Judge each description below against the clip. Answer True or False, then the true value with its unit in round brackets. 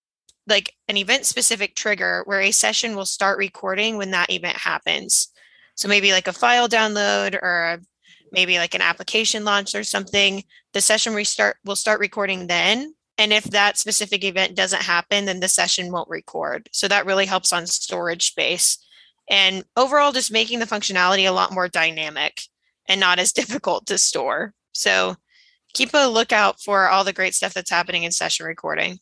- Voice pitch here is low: False (200 Hz)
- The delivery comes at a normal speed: True (175 wpm)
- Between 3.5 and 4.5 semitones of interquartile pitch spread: False (2.9 semitones)